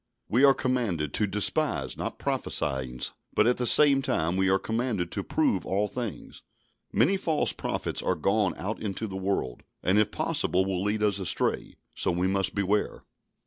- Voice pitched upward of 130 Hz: No, low, 100 Hz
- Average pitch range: Yes, average, 3.7 semitones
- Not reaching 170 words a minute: No, average, 175 wpm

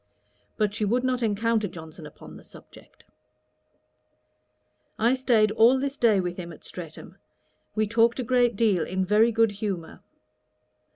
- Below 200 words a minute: Yes, average, 150 wpm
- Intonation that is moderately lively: Yes, average, 3.7 semitones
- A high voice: Yes, high, 215 Hz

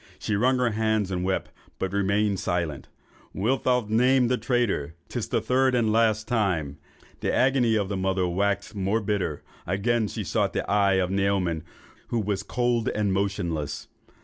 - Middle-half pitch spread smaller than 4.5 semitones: Yes, average, 3.5 semitones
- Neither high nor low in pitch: No, low, 100 Hz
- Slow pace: No, average, 175 wpm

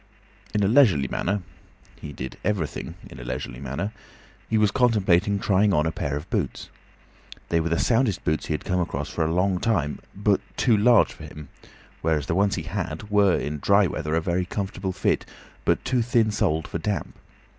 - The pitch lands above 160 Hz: No, very low, 90 Hz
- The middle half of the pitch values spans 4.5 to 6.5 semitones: Yes, average, 4.8 semitones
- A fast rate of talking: No, average, 190 wpm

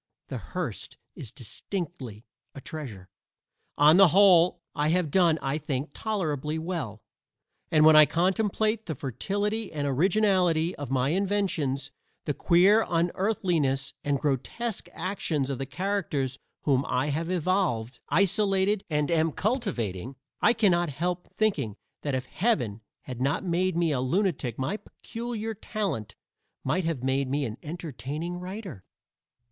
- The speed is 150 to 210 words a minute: No, slow, 135 wpm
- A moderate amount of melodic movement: No, wide, 5.9 semitones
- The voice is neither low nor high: Yes, medium, 165 Hz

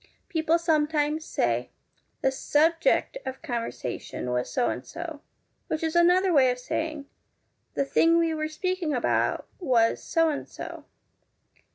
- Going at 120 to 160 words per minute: Yes, average, 150 wpm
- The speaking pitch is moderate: No, very high, 310 Hz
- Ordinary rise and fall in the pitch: Yes, average, 3.8 semitones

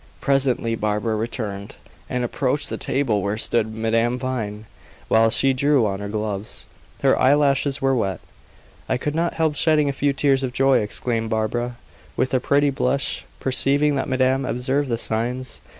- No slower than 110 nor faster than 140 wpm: No, average, 165 wpm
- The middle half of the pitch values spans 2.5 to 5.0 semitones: Yes, average, 3.7 semitones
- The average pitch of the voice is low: Yes, low, 125 Hz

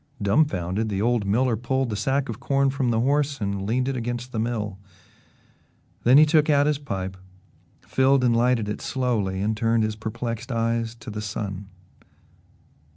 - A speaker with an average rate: Yes, average, 170 wpm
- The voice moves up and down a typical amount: Yes, average, 3.8 semitones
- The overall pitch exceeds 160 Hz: No, low, 115 Hz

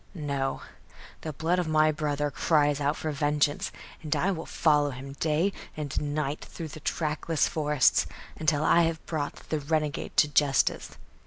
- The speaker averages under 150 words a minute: No, average, 160 wpm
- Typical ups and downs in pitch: No, narrow, 1.5 semitones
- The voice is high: No, medium, 150 Hz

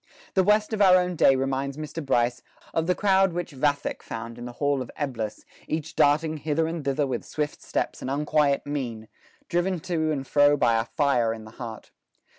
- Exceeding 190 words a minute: Yes, fast, 205 wpm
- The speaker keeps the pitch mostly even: No, average, 3.9 semitones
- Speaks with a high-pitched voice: No, medium, 145 Hz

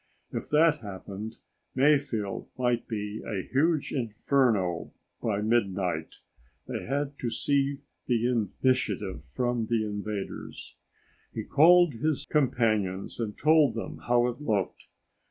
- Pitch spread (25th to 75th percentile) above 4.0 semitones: Yes, average, 5.1 semitones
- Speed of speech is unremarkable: No, slow, 120 wpm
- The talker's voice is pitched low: Yes, low, 120 Hz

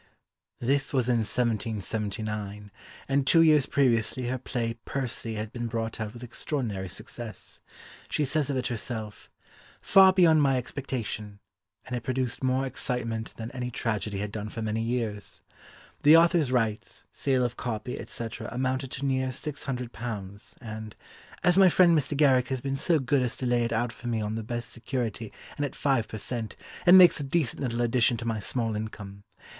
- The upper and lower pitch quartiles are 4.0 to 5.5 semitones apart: No, average, 3.4 semitones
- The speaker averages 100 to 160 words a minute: No, average, 180 wpm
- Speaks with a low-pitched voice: Yes, low, 120 Hz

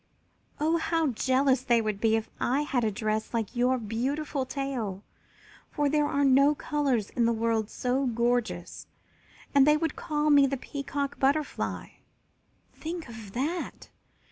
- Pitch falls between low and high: No, very high, 265 Hz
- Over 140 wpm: Yes, average, 150 wpm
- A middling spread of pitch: Yes, average, 4.1 semitones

